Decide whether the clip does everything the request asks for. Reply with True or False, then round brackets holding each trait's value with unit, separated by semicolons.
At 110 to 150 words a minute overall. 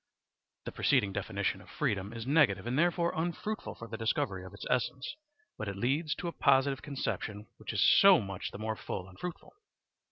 False (190 wpm)